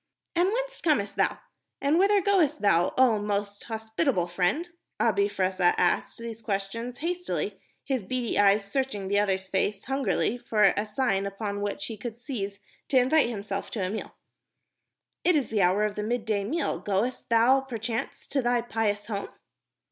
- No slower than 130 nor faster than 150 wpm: No, average, 170 wpm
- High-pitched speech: Yes, high, 220 Hz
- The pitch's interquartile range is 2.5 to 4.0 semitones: No, average, 4.5 semitones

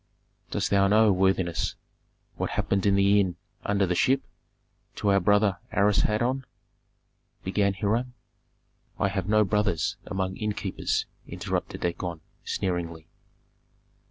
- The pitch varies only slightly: Yes, narrow, 1.9 semitones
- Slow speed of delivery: Yes, slow, 115 wpm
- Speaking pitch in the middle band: No, low, 100 Hz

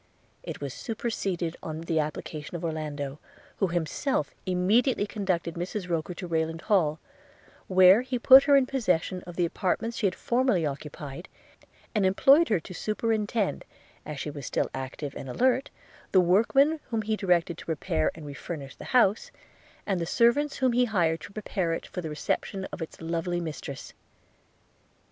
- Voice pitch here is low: No, medium, 180 Hz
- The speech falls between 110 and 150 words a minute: No, average, 165 wpm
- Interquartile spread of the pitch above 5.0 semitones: Yes, wide, 5.4 semitones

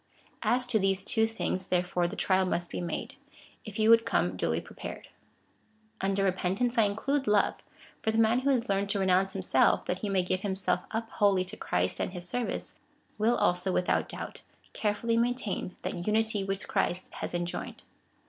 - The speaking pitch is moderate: No, high, 195 Hz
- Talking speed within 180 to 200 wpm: Yes, average, 185 wpm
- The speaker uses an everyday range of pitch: Yes, average, 3.5 semitones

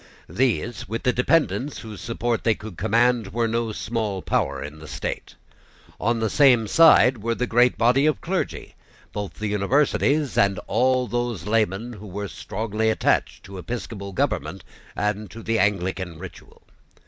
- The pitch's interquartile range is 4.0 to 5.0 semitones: No, average, 3.2 semitones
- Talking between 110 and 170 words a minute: Yes, average, 160 wpm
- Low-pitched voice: Yes, low, 115 Hz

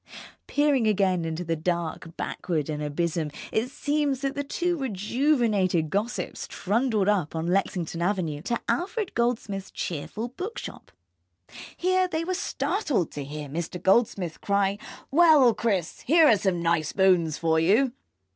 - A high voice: Yes, high, 200 Hz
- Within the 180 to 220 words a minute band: No, average, 140 wpm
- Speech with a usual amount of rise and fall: No, wide, 8.0 semitones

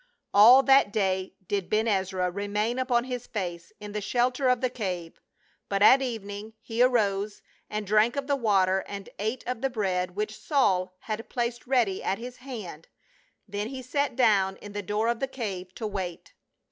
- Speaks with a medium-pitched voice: No, high, 215 Hz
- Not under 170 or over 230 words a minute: Yes, average, 185 wpm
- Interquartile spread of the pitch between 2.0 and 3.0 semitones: No, average, 4.0 semitones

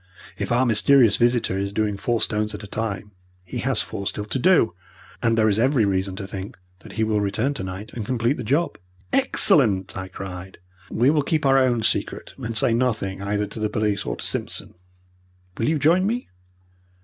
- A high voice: No, low, 110 Hz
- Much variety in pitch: No, average, 3.9 semitones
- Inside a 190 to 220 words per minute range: Yes, average, 195 wpm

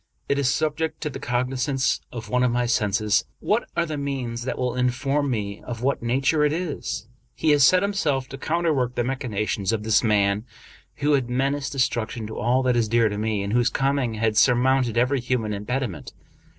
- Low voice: Yes, low, 125 Hz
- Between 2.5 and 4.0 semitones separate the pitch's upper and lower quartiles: Yes, average, 3.6 semitones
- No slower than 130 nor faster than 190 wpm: No, fast, 205 wpm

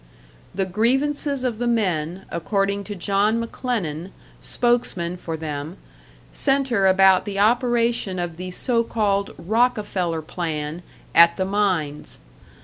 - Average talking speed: No, slow, 120 wpm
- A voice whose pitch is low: No, high, 195 Hz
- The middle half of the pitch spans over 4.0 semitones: Yes, average, 5.1 semitones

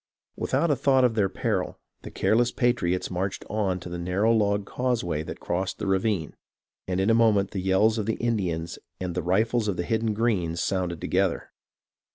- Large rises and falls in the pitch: No, average, 3.8 semitones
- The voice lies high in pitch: No, low, 100 Hz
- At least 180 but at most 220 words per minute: Yes, average, 190 wpm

